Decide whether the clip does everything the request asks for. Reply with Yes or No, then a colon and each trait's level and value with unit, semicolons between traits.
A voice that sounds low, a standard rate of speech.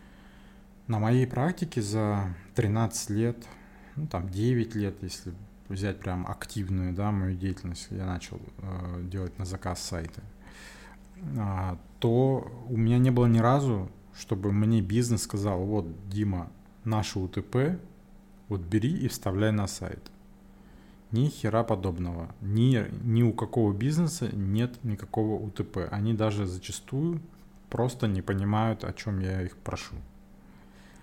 Yes: low, 105 Hz; average, 130 wpm